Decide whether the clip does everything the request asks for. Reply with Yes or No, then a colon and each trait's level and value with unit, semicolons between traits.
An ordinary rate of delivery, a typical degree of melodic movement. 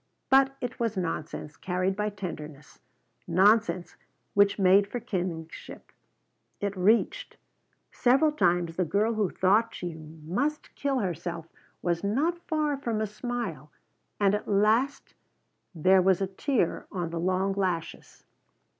No: slow, 130 wpm; average, 4.7 semitones